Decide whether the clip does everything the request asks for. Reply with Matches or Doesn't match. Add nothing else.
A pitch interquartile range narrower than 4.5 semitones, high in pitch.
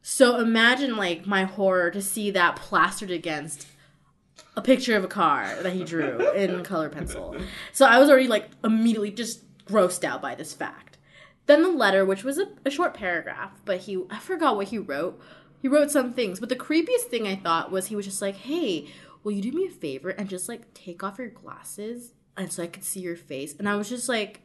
Doesn't match